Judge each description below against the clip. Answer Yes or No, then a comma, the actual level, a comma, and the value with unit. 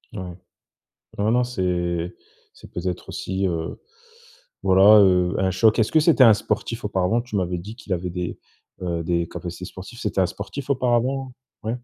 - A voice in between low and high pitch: No, very low, 95 Hz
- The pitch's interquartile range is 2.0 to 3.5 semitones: No, average, 4.4 semitones